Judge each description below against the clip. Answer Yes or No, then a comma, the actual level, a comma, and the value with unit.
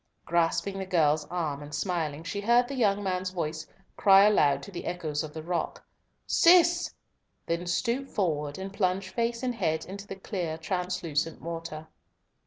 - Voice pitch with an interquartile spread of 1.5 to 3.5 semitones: No, average, 4.1 semitones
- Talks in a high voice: No, medium, 180 Hz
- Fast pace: No, average, 165 wpm